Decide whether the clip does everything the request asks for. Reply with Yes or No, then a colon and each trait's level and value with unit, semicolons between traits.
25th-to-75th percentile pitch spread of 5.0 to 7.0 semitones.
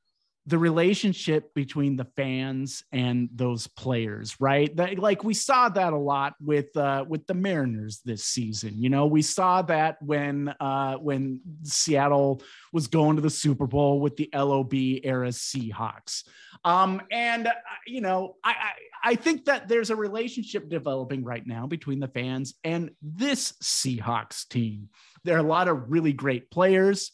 Yes: wide, 5.6 semitones